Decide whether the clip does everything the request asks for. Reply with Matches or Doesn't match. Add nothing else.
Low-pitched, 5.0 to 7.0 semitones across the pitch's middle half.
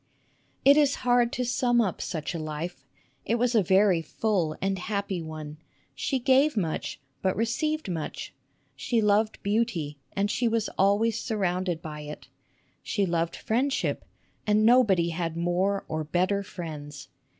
Doesn't match